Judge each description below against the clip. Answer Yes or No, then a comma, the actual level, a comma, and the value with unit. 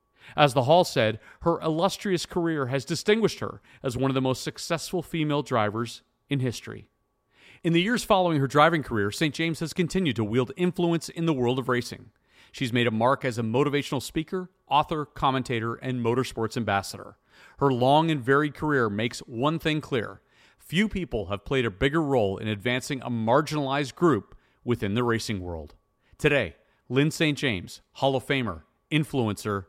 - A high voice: No, low, 135 Hz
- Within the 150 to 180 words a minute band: Yes, average, 170 wpm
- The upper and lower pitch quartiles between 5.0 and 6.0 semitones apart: Yes, average, 5.3 semitones